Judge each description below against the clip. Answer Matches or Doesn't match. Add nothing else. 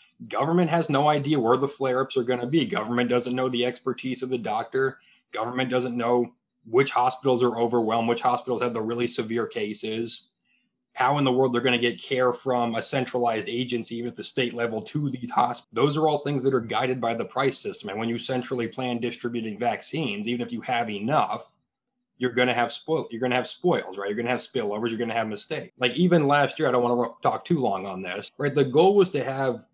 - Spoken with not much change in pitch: Matches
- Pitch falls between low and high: Doesn't match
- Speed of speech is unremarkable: Doesn't match